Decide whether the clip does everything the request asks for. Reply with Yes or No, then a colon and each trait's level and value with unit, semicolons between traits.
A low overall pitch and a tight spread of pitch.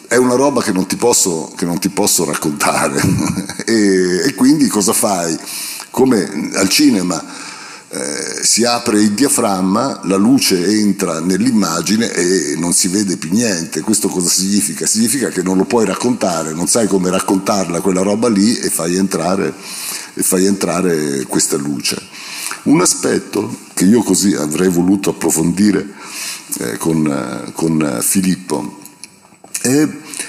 Yes: very low, 95 Hz; narrow, 1.9 semitones